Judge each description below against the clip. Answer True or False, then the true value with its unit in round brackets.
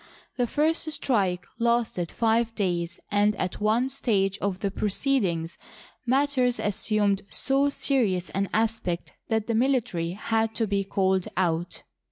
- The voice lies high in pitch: True (215 Hz)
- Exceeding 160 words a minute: False (140 wpm)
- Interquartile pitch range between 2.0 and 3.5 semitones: False (4.3 semitones)